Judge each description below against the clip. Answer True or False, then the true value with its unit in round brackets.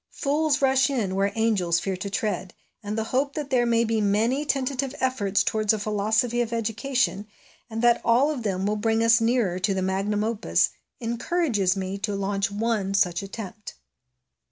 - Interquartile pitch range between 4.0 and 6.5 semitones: False (3.5 semitones)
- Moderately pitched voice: False (220 Hz)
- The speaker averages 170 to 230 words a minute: True (180 wpm)